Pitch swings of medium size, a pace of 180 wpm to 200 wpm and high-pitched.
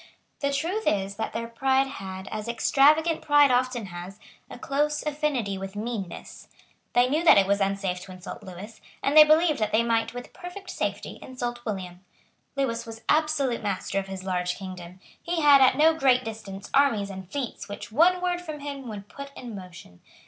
No: wide, 6.6 semitones; average, 185 wpm; high, 235 Hz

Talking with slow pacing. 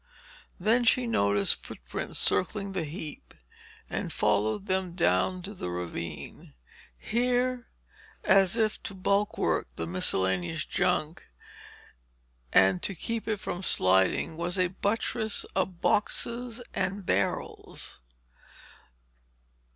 Yes: slow, 105 wpm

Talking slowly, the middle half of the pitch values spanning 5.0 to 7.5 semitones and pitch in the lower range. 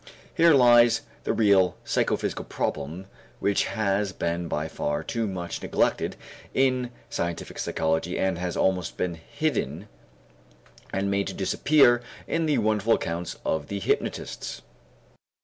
Yes: slow, 130 wpm; wide, 5.6 semitones; low, 100 Hz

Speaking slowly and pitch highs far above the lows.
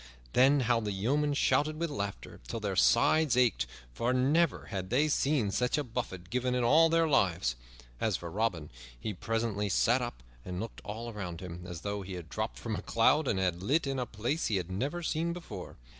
No: fast, 205 wpm; wide, 6.8 semitones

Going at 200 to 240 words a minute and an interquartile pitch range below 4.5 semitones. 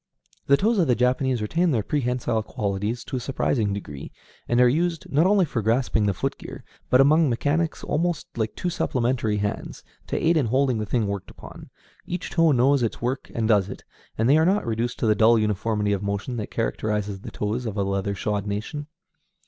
No: fast, 205 wpm; average, 5.1 semitones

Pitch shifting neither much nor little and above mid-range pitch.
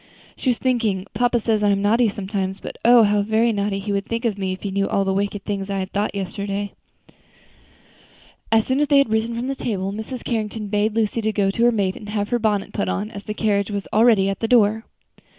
No: narrow, 2.3 semitones; high, 210 Hz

